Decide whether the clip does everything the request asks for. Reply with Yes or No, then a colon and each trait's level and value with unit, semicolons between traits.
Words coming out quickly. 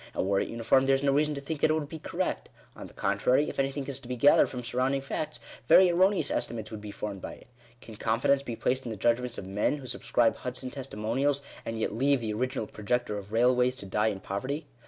Yes: fast, 240 wpm